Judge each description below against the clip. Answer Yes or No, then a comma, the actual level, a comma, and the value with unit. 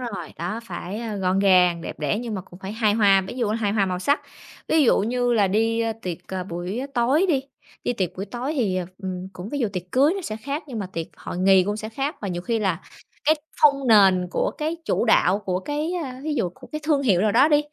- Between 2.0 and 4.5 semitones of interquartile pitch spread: No, wide, 5.4 semitones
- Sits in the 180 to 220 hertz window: Yes, high, 215 Hz